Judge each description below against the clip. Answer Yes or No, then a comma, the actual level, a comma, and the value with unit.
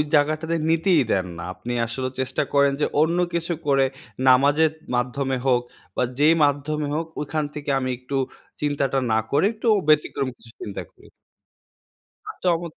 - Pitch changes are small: No, average, 3.2 semitones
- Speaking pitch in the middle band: Yes, medium, 145 Hz